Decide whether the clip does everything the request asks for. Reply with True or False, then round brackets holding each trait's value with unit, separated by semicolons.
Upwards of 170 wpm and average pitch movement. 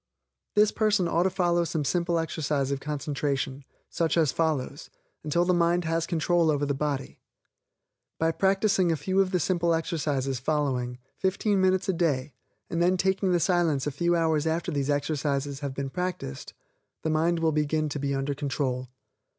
True (180 wpm; 3.5 semitones)